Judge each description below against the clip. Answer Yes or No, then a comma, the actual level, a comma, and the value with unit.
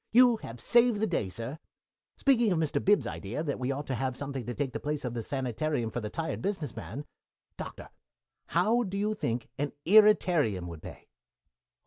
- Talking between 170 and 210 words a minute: Yes, average, 190 wpm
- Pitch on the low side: No, medium, 145 Hz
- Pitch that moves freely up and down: Yes, wide, 8.9 semitones